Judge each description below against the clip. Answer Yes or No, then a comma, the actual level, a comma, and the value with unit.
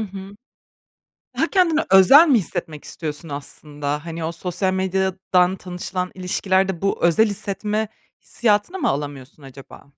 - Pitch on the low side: No, medium, 185 Hz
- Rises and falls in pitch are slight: No, average, 3.8 semitones